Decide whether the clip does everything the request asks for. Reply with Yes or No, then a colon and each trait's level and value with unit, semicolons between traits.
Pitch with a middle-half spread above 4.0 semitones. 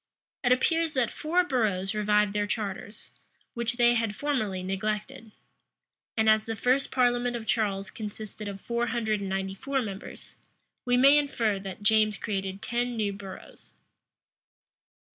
No: average, 3.3 semitones